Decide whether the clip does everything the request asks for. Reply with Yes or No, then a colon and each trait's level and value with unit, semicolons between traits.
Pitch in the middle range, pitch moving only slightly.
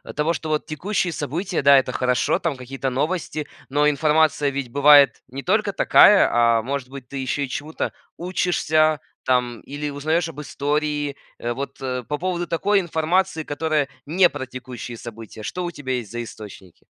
No: medium, 145 Hz; average, 3.7 semitones